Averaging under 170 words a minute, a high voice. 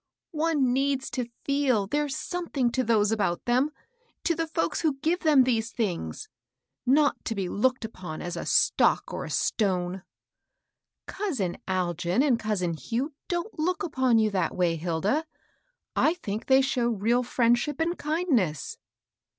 Yes: average, 160 wpm; very high, 250 Hz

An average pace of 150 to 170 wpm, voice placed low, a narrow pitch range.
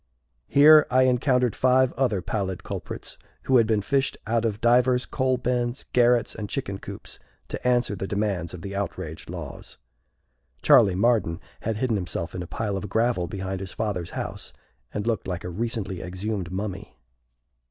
No: average, 165 wpm; low, 110 Hz; average, 4.6 semitones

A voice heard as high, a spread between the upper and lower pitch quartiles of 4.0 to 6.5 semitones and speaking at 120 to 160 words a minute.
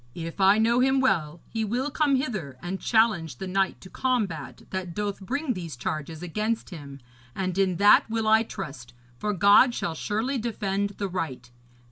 No: high, 195 Hz; average, 5.1 semitones; average, 175 wpm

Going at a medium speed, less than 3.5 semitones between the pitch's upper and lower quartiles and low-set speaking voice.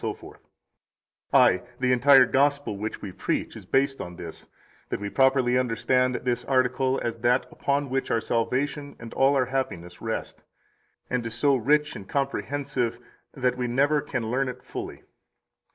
Yes: average, 165 wpm; average, 2.7 semitones; low, 130 Hz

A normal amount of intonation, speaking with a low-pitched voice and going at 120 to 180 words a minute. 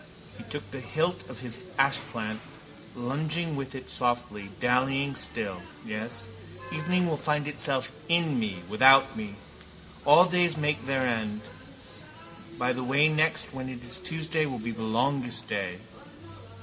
Yes: average, 4.4 semitones; low, 130 Hz; average, 145 wpm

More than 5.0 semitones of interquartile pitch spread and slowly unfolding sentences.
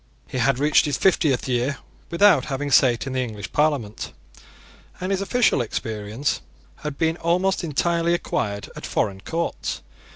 No: wide, 5.6 semitones; average, 150 wpm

